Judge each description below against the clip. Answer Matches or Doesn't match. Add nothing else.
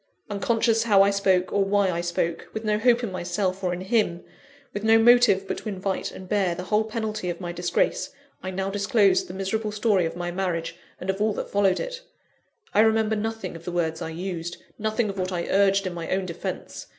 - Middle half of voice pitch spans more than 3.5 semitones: Doesn't match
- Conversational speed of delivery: Doesn't match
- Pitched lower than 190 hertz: Doesn't match